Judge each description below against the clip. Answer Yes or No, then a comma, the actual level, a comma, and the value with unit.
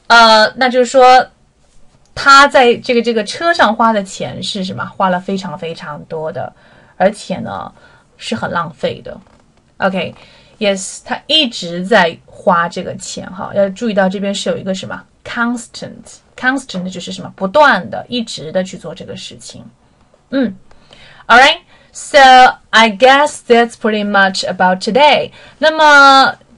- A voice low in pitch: No, high, 220 Hz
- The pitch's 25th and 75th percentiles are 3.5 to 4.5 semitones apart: No, average, 5.3 semitones